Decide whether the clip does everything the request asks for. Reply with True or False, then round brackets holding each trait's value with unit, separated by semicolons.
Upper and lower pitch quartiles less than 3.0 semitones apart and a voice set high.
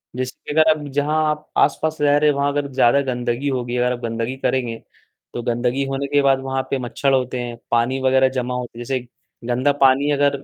False (2.5 semitones; 130 Hz)